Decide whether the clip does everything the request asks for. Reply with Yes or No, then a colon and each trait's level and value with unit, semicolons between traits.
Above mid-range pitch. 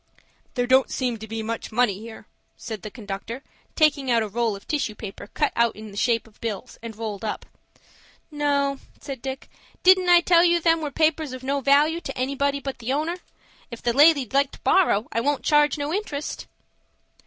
Yes: very high, 265 Hz